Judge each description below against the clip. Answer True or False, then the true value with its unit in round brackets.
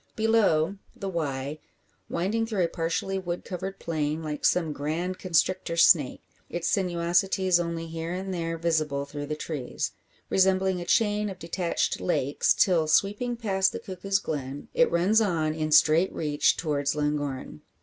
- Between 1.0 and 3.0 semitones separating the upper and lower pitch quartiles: False (3.7 semitones)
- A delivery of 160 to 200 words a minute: False (150 wpm)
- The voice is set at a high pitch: False (170 Hz)